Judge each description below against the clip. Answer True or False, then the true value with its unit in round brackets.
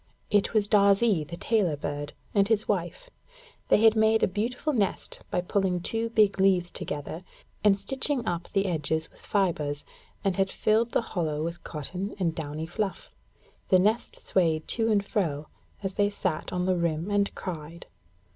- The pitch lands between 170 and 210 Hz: True (190 Hz)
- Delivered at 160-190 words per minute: True (175 wpm)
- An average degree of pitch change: True (4.1 semitones)